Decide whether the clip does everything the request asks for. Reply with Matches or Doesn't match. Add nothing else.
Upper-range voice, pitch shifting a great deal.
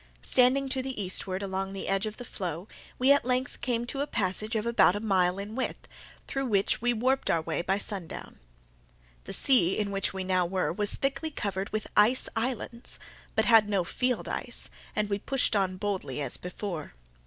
Doesn't match